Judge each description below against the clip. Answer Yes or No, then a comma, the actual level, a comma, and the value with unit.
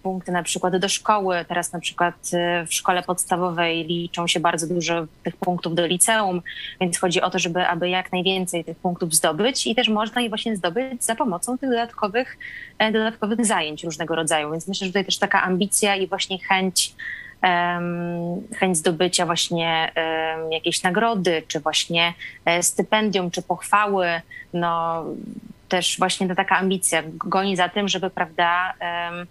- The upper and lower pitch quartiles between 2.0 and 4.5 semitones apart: Yes, narrow, 2.6 semitones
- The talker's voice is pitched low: No, medium, 180 Hz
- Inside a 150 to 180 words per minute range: Yes, average, 155 wpm